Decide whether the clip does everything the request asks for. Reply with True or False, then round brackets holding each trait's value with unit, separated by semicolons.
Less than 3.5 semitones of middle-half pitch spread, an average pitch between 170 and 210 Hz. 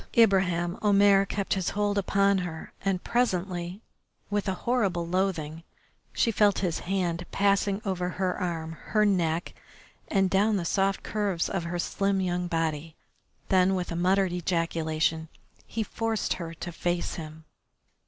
True (2.6 semitones; 185 Hz)